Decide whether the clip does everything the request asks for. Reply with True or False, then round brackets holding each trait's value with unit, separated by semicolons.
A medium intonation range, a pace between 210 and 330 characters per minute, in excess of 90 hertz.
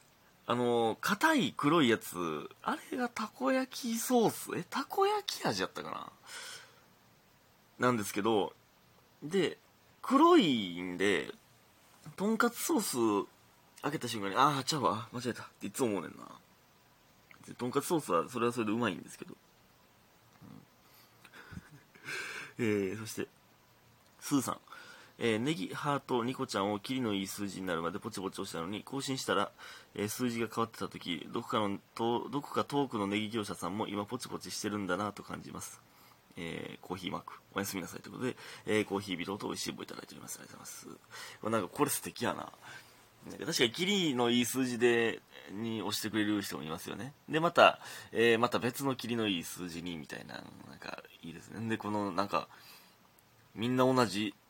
False (5.0 semitones; 345 characters per minute; 115 Hz)